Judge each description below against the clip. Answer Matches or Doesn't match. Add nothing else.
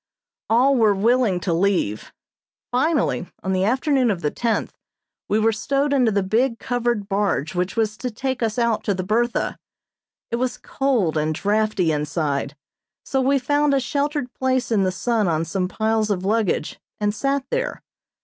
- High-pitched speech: Matches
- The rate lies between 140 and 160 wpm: Doesn't match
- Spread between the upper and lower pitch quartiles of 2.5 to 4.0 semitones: Doesn't match